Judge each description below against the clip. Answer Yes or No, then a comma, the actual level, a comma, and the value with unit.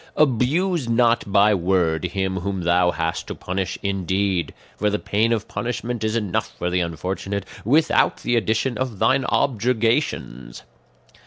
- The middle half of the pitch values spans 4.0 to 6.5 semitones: Yes, average, 4.4 semitones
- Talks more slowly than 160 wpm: Yes, average, 150 wpm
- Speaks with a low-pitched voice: Yes, low, 105 Hz